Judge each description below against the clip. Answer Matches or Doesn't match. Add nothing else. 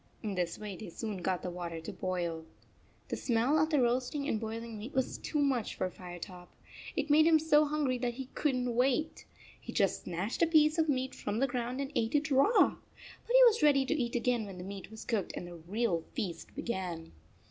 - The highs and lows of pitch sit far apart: Matches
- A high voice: Matches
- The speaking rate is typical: Doesn't match